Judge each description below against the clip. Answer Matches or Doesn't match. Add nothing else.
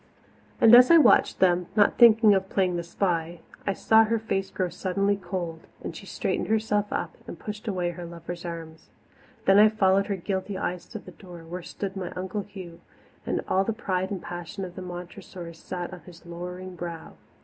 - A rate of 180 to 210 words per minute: Matches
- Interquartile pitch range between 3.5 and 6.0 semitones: Doesn't match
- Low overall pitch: Doesn't match